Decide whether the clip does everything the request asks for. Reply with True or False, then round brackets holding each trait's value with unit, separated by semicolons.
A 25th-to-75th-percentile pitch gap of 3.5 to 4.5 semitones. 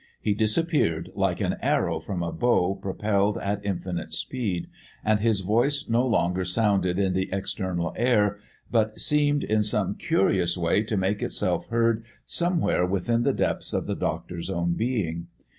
True (4.2 semitones)